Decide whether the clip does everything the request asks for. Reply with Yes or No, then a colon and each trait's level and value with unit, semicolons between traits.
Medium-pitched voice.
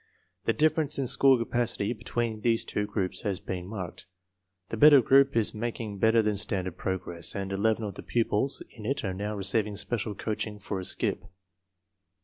No: low, 105 Hz